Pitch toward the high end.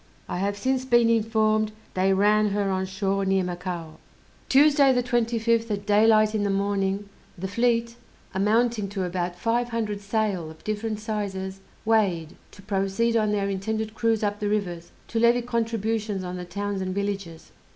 Yes: high, 205 Hz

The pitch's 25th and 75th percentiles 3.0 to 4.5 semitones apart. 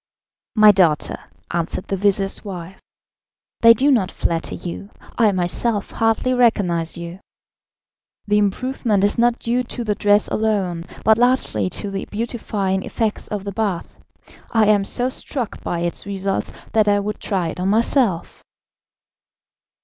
Yes: average, 3.3 semitones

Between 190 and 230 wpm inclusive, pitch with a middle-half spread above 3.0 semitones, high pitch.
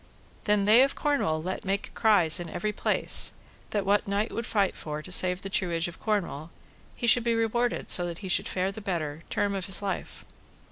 Yes: fast, 205 wpm; average, 3.4 semitones; high, 195 Hz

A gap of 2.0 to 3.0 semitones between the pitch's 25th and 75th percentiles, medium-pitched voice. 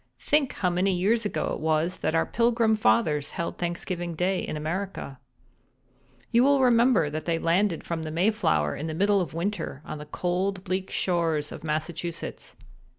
No: average, 4.1 semitones; medium, 175 Hz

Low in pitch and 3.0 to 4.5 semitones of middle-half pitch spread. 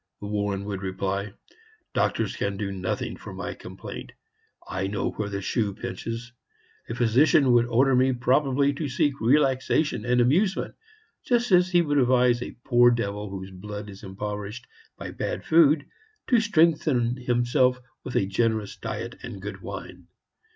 No: low, 120 Hz; average, 5.1 semitones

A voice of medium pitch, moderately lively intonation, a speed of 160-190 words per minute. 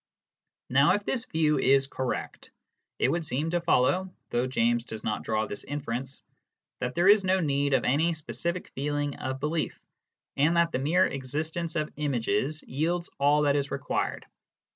Yes: medium, 145 Hz; average, 4.0 semitones; average, 165 wpm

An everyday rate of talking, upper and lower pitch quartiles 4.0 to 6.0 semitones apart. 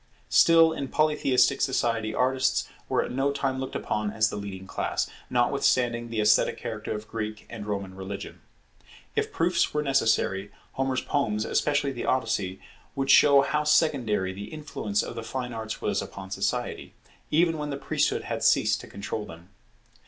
Yes: average, 165 wpm; average, 4.8 semitones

